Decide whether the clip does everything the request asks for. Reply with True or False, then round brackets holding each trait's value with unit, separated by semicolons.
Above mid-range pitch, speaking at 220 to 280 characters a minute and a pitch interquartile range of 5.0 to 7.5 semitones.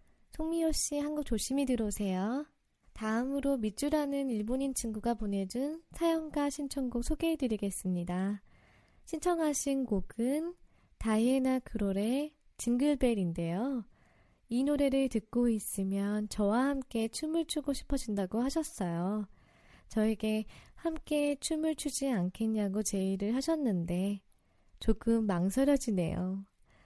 True (240 Hz; 265 characters per minute; 5.6 semitones)